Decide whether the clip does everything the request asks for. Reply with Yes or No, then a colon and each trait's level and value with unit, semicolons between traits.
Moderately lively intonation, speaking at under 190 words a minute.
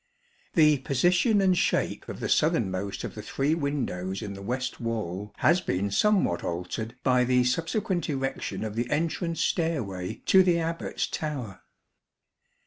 No: wide, 8.6 semitones; average, 145 wpm